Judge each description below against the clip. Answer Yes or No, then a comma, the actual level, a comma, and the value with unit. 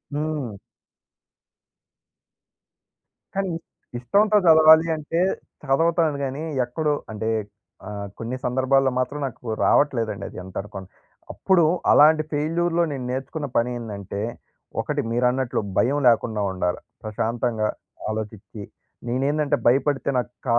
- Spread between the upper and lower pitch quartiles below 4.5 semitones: No, average, 5.1 semitones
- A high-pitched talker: No, low, 130 Hz